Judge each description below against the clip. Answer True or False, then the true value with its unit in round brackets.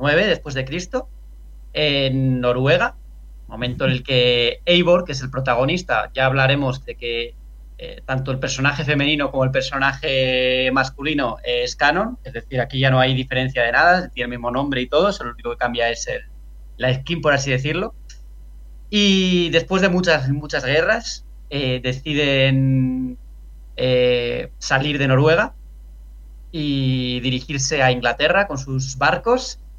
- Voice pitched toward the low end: True (130 Hz)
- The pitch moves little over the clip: False (3.5 semitones)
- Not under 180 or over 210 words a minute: False (155 wpm)